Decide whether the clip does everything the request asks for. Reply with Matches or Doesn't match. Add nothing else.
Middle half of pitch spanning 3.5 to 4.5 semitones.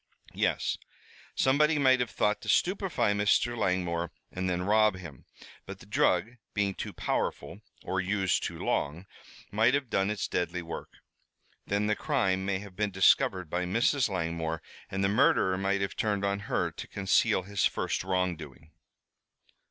Doesn't match